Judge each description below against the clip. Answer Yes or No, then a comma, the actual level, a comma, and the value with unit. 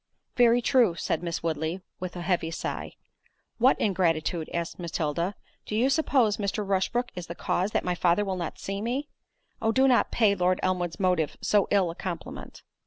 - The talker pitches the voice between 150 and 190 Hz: Yes, medium, 185 Hz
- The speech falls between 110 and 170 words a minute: No, average, 180 wpm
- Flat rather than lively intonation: No, average, 4.4 semitones